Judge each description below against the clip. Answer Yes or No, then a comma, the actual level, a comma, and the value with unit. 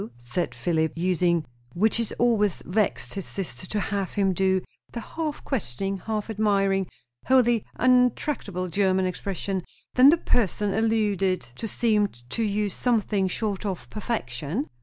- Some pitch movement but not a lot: Yes, average, 3.3 semitones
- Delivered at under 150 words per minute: Yes, average, 140 wpm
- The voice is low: No, high, 200 Hz